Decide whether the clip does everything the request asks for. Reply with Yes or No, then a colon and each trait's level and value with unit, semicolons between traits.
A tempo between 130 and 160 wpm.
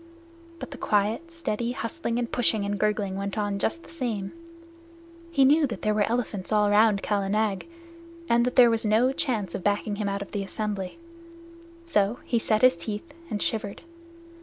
No: average, 185 wpm